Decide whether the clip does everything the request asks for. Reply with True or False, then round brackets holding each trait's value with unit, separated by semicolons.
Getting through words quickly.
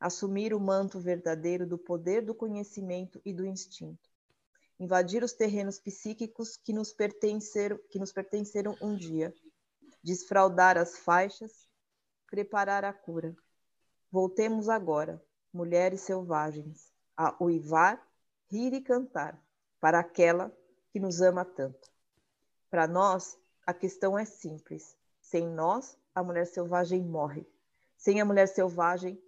False (125 wpm)